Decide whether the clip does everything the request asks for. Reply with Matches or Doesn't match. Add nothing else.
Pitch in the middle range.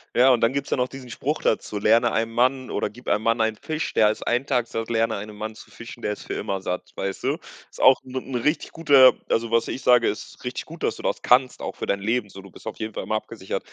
Doesn't match